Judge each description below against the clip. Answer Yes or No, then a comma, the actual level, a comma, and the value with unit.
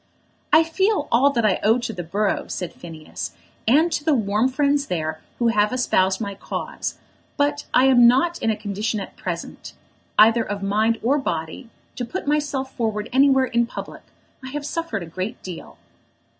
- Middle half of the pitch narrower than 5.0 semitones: No, wide, 5.5 semitones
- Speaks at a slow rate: No, average, 180 wpm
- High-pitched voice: Yes, high, 235 Hz